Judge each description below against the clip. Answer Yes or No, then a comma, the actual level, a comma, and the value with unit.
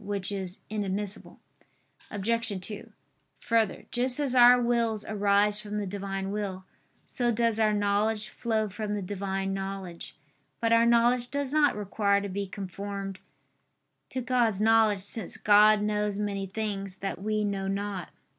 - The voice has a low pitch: No, high, 205 Hz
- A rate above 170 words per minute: No, average, 145 wpm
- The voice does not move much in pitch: Yes, narrow, 2.2 semitones